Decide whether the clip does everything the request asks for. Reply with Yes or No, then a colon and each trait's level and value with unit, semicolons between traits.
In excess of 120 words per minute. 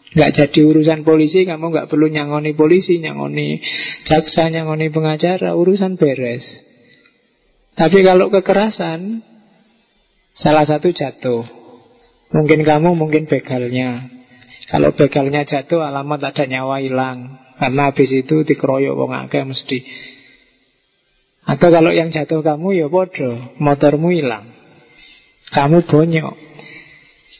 No: average, 110 wpm